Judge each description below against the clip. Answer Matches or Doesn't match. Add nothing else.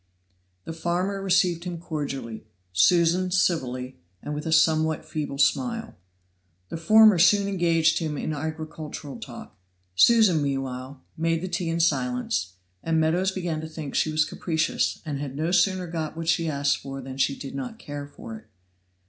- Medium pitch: Matches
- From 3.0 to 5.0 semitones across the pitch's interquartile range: Matches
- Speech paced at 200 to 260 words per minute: Doesn't match